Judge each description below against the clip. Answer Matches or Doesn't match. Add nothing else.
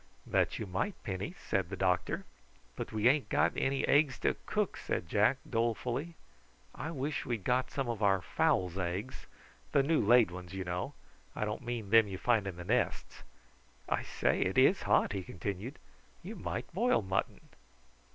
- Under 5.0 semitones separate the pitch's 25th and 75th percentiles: Doesn't match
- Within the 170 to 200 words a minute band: Matches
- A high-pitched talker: Doesn't match